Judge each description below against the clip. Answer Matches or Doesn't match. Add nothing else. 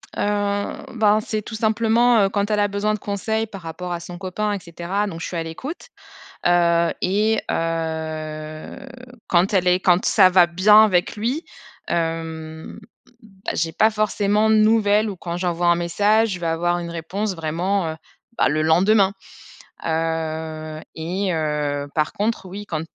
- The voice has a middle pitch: Matches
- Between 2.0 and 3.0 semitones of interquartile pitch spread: Doesn't match